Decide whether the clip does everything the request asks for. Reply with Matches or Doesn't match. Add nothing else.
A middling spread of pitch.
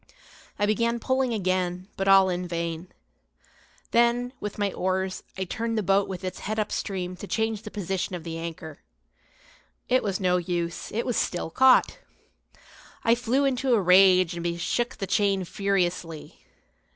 Matches